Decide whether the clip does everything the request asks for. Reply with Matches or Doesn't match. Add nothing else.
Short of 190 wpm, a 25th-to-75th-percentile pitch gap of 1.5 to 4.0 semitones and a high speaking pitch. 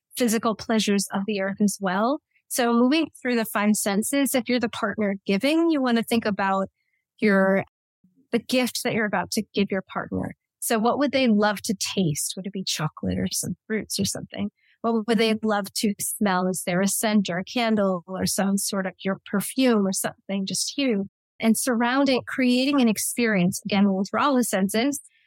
Doesn't match